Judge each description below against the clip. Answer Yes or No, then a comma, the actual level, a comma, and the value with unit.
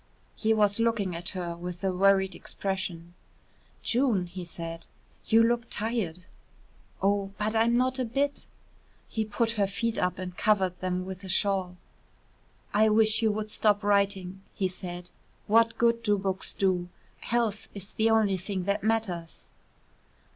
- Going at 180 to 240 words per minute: No, average, 155 wpm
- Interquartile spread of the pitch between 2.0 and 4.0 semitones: Yes, average, 3.3 semitones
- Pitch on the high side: Yes, high, 200 Hz